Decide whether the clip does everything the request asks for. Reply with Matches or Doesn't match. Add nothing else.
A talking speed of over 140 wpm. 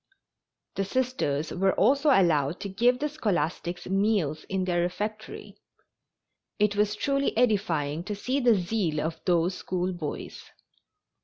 Doesn't match